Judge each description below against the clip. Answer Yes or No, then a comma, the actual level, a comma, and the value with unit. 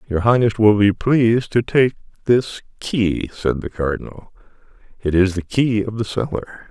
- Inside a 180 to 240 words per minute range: No, average, 170 wpm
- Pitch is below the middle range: Yes, low, 110 Hz